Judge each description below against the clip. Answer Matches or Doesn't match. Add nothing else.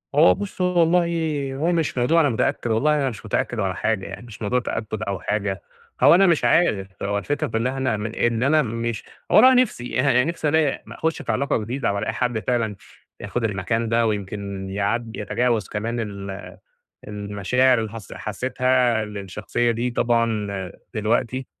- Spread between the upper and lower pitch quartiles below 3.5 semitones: Doesn't match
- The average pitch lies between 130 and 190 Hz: Doesn't match